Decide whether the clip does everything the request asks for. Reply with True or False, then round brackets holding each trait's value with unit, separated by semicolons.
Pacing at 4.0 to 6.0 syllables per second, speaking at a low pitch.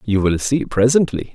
True (4.8 syllables/s; 120 Hz)